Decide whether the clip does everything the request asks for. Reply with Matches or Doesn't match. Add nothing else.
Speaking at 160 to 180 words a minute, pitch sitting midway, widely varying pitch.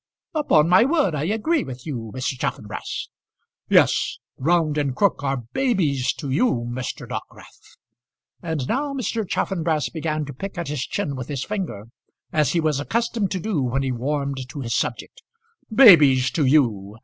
Matches